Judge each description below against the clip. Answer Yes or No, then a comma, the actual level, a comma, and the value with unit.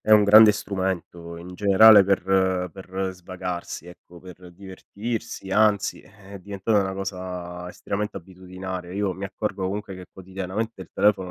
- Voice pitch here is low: Yes, very low, 95 Hz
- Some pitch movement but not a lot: No, narrow, 1.9 semitones